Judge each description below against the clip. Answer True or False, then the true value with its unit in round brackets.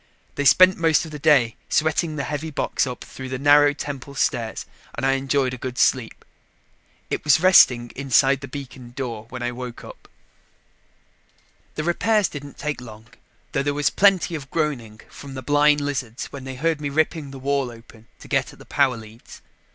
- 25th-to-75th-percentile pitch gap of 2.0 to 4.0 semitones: True (3.1 semitones)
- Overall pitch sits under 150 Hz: True (140 Hz)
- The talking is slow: False (190 wpm)